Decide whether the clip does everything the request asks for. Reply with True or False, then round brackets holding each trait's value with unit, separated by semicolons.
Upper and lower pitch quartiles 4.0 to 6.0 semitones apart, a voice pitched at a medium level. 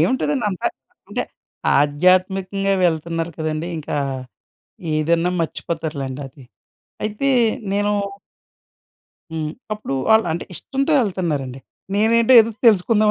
True (5.2 semitones; 175 Hz)